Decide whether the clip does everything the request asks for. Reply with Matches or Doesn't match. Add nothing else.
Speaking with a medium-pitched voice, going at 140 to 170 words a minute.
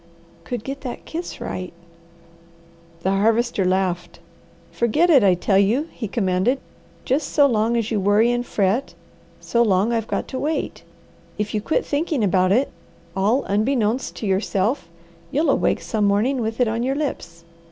Doesn't match